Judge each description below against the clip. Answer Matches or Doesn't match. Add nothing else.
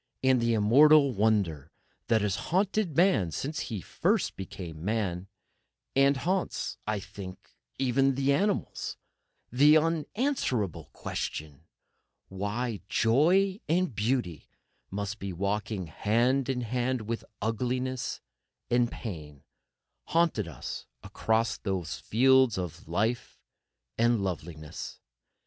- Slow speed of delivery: Matches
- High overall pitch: Doesn't match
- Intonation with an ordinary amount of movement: Doesn't match